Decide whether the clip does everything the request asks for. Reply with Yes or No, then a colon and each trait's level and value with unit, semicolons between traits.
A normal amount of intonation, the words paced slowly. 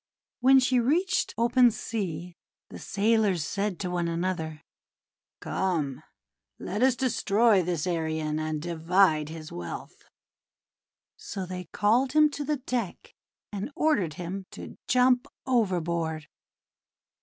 No: wide, 6.6 semitones; slow, 120 wpm